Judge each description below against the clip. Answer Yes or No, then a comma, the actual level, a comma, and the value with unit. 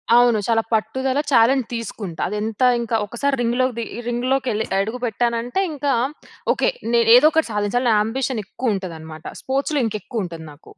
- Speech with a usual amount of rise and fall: Yes, average, 3.3 semitones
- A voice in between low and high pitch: No, high, 235 Hz